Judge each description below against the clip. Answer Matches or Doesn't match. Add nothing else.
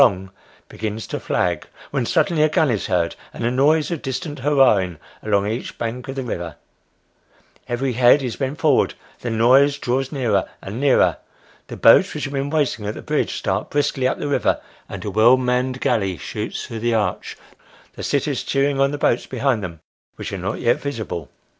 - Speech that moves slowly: Doesn't match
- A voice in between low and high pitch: Doesn't match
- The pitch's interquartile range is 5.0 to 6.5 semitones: Doesn't match